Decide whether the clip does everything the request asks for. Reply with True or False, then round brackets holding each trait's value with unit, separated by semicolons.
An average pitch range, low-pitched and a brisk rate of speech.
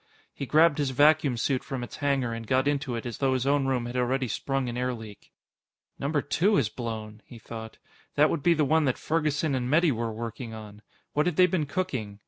True (3.9 semitones; 130 Hz; 225 wpm)